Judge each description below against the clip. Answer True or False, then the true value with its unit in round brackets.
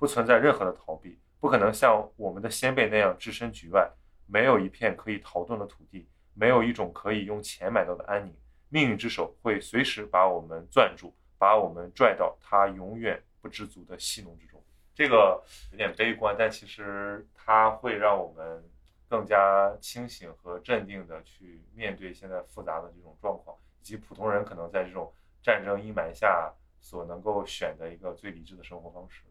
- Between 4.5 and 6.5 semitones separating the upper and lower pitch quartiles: False (3.9 semitones)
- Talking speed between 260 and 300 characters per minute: True (285 characters per minute)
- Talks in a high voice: False (95 Hz)